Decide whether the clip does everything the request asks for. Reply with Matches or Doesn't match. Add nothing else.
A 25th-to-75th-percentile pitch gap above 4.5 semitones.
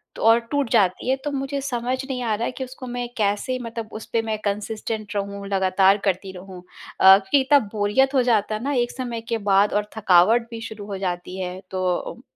Doesn't match